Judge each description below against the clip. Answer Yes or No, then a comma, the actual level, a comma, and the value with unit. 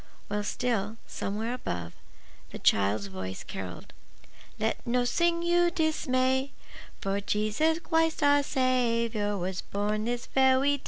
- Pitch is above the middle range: Yes, high, 235 Hz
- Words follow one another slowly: Yes, slow, 130 wpm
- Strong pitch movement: Yes, wide, 5.7 semitones